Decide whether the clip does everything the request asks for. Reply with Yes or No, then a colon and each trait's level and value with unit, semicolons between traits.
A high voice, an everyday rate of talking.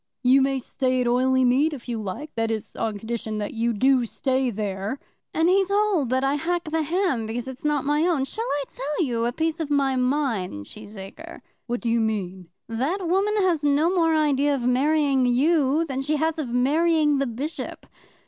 Yes: very high, 270 Hz; average, 195 wpm